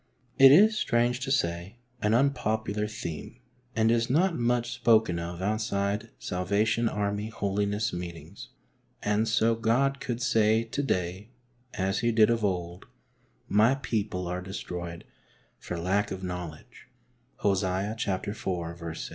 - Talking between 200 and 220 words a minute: No, average, 140 wpm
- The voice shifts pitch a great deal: No, average, 4.1 semitones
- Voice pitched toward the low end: Yes, low, 105 Hz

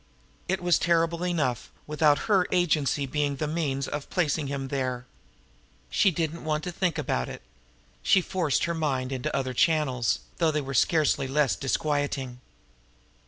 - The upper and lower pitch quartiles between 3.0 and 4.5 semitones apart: Yes, average, 3.7 semitones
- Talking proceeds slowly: No, average, 160 wpm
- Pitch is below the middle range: No, medium, 150 Hz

